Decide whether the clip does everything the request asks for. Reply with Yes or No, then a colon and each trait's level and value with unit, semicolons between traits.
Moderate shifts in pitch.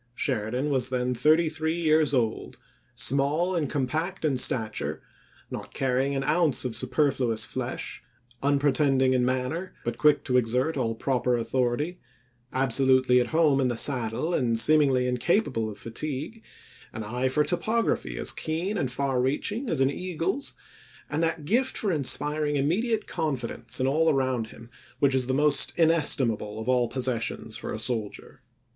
Yes: average, 3.9 semitones